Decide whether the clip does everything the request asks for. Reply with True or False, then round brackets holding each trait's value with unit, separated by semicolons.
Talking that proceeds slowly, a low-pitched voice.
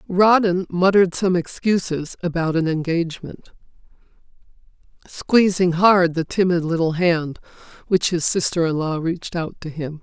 False (130 wpm; 175 Hz)